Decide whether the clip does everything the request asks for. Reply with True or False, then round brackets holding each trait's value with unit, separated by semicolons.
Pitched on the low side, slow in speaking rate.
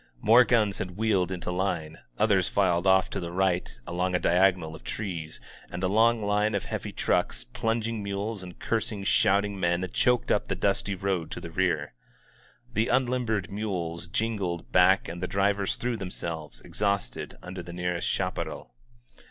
False (95 Hz; 165 wpm)